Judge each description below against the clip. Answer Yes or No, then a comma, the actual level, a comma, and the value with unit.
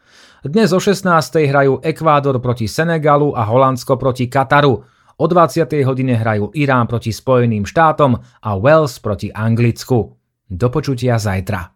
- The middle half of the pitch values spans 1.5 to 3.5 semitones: No, average, 4.5 semitones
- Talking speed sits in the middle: Yes, average, 125 wpm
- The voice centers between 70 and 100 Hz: No, low, 130 Hz